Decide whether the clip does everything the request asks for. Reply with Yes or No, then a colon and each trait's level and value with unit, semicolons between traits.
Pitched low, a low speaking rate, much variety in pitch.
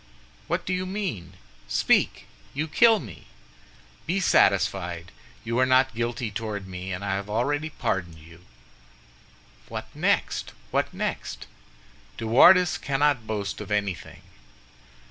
Yes: low, 110 Hz; slow, 125 wpm; wide, 7.2 semitones